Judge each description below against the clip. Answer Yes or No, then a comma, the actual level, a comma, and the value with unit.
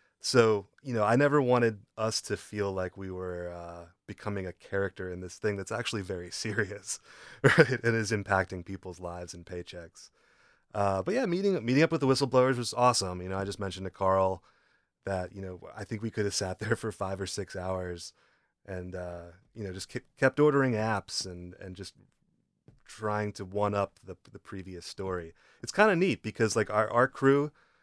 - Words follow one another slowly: No, average, 200 wpm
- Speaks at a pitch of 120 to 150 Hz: No, low, 100 Hz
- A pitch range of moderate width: Yes, average, 3.8 semitones